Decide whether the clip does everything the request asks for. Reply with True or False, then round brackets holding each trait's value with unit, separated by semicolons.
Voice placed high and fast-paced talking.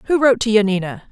True (220 Hz; 215 wpm)